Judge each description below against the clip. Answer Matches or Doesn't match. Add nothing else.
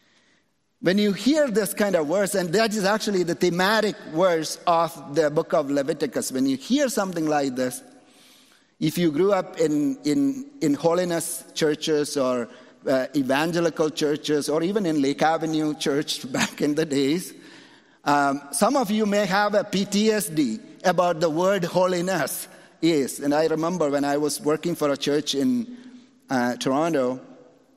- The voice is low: Doesn't match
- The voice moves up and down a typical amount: Doesn't match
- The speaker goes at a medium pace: Matches